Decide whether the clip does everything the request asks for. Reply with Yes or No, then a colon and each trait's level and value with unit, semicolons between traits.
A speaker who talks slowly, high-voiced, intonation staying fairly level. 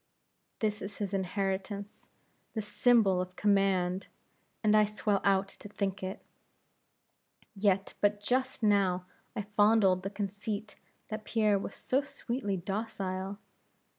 Yes: slow, 125 wpm; high, 200 Hz; narrow, 1.7 semitones